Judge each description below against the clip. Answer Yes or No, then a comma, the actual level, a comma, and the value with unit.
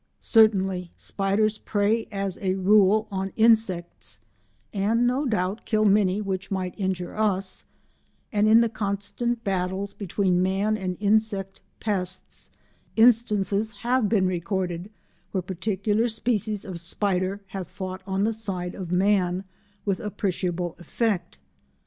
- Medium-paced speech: No, slow, 125 wpm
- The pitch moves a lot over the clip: No, narrow, 2.5 semitones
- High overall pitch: Yes, high, 195 Hz